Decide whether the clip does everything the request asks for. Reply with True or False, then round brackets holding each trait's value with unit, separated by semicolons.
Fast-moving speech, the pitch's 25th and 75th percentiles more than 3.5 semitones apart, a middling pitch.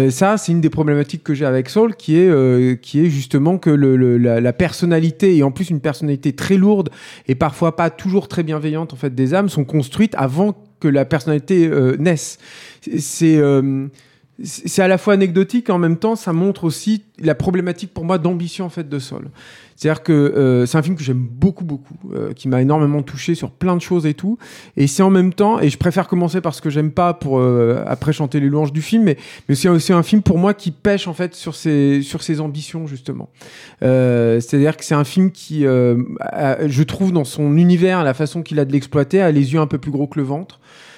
True (235 wpm; 4.1 semitones; 155 Hz)